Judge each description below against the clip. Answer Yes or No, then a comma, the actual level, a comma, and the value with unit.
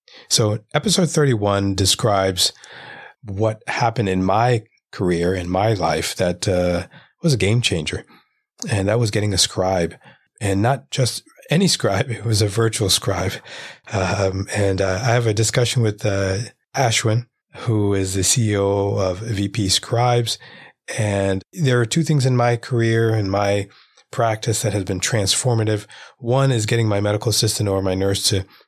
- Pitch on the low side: Yes, low, 105 Hz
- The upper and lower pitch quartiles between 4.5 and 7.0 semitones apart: No, average, 3.3 semitones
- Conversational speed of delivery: Yes, average, 160 wpm